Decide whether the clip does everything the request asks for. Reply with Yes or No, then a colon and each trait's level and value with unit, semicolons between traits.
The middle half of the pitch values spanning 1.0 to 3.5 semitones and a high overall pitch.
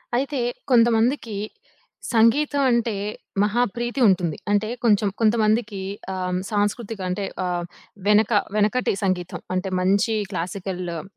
No: average, 3.9 semitones; high, 210 Hz